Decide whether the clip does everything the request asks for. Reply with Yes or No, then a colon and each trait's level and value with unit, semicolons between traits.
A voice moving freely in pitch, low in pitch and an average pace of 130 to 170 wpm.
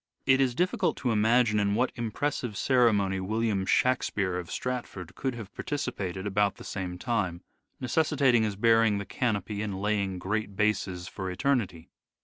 No: average, 4.1 semitones; low, 105 Hz; average, 150 wpm